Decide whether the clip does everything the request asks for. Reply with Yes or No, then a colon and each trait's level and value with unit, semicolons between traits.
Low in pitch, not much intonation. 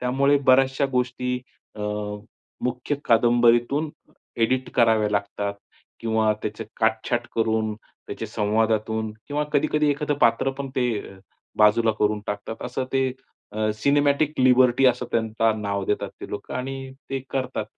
No: low, 120 Hz; average, 3.3 semitones